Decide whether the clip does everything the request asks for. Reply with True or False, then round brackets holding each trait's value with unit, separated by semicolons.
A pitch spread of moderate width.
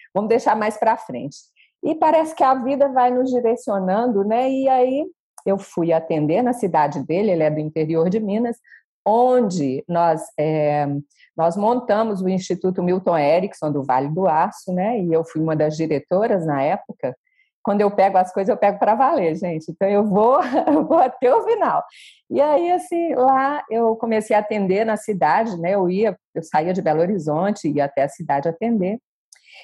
False (6.8 semitones)